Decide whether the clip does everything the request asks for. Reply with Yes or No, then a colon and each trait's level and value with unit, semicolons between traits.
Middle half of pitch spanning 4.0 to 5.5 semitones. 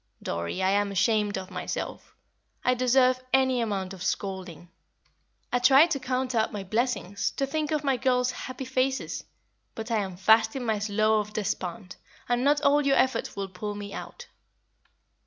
Yes: average, 4.6 semitones